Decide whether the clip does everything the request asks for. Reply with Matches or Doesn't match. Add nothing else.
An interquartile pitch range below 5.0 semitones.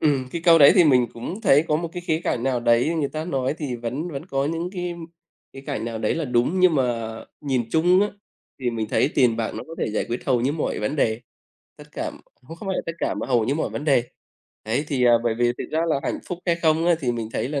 Doesn't match